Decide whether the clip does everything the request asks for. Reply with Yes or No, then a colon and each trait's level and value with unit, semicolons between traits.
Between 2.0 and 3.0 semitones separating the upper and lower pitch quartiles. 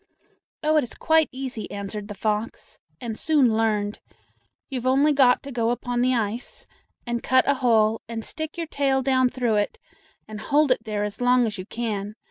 No: average, 3.6 semitones